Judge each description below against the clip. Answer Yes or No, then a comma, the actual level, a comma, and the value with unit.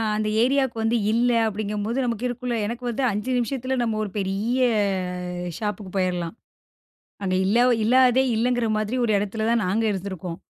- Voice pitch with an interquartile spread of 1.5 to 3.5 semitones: Yes, average, 3.2 semitones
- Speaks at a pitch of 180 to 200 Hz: No, high, 225 Hz